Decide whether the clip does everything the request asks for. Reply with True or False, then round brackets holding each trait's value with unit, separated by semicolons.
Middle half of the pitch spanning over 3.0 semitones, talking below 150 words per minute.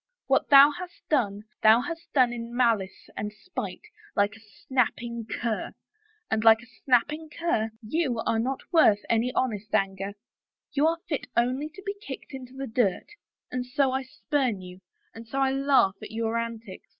False (3.9 semitones; 175 wpm)